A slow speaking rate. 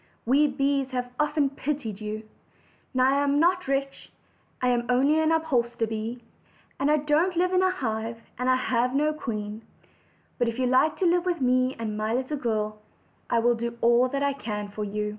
No: average, 200 wpm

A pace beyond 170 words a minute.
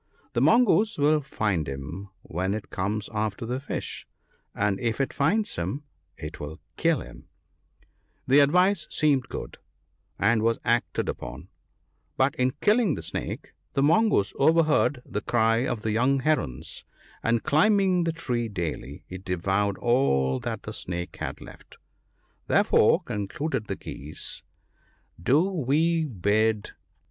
No: average, 140 wpm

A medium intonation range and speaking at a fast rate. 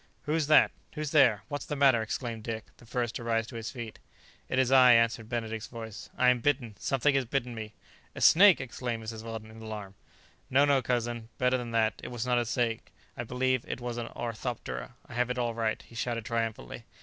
No: narrow, 2.1 semitones; fast, 215 wpm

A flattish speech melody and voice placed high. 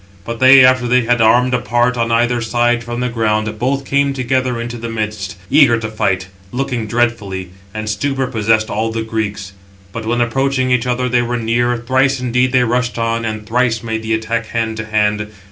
No: narrow, 2.2 semitones; low, 115 Hz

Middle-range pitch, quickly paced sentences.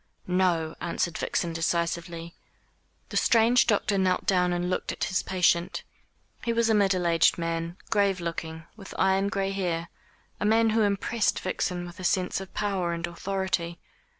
No: medium, 180 Hz; average, 160 wpm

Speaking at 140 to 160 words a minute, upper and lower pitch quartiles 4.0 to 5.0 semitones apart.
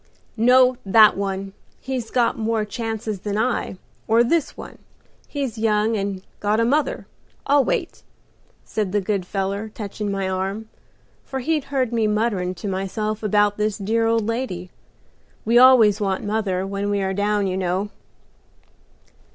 No: average, 155 wpm; narrow, 2.6 semitones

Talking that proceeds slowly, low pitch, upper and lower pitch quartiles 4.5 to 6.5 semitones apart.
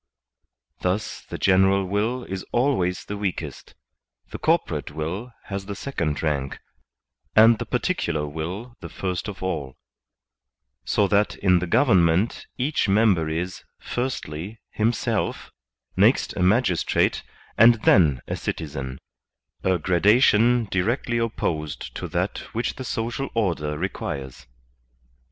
Yes: slow, 125 wpm; very low, 95 Hz; wide, 5.6 semitones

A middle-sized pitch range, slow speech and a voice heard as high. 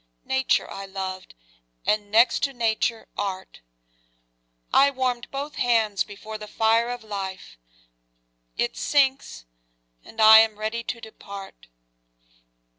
Yes: average, 3.4 semitones; slow, 115 wpm; high, 220 Hz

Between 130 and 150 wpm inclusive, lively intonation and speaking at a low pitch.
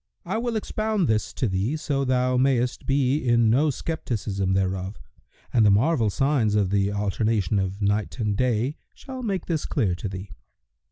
No: average, 170 wpm; wide, 5.9 semitones; low, 120 Hz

